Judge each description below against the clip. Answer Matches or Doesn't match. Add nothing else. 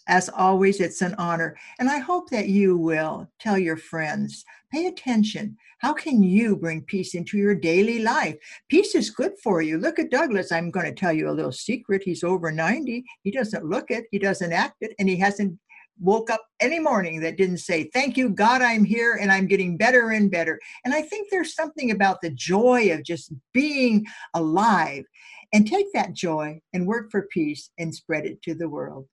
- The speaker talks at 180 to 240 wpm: Matches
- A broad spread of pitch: Matches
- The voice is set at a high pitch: Matches